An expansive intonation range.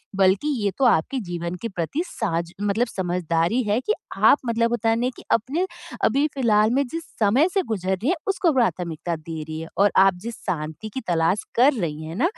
Yes: wide, 6.2 semitones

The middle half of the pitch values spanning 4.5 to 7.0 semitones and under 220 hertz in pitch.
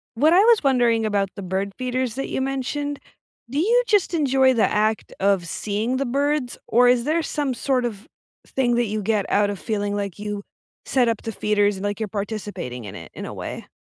No: average, 4.8 semitones; high, 230 Hz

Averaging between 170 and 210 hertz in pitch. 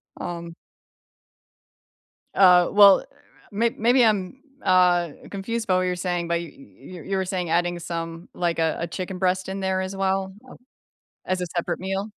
Yes: medium, 185 Hz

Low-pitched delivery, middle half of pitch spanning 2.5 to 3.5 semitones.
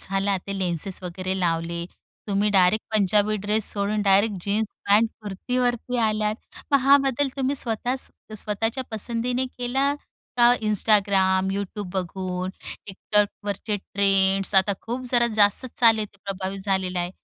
No: high, 205 Hz; average, 2.9 semitones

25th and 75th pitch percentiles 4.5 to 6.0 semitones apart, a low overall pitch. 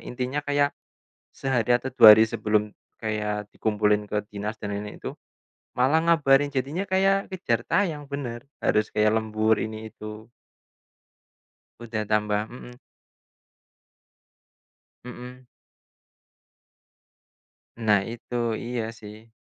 No: average, 4.1 semitones; low, 115 Hz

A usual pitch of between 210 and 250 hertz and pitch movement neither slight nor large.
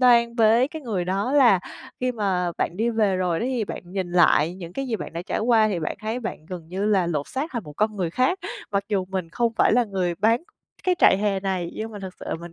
No: high, 200 Hz; average, 4.5 semitones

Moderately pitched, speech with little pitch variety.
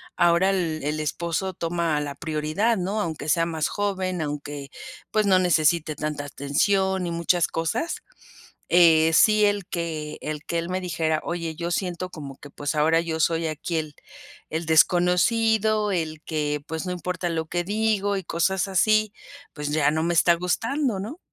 No: medium, 170 Hz; average, 3.3 semitones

